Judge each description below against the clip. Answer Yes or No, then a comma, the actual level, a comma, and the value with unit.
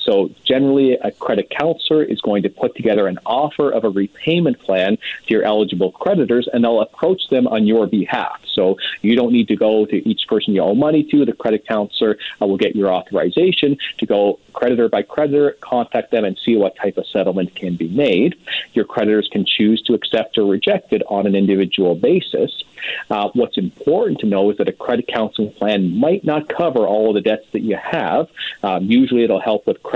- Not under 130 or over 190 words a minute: No, fast, 205 wpm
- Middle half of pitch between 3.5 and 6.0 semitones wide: Yes, average, 5.2 semitones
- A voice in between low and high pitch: No, low, 115 Hz